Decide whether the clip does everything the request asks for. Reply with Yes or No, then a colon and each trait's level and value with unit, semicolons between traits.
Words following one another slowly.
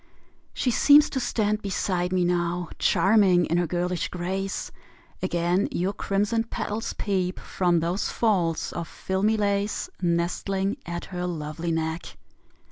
Yes: slow, 130 wpm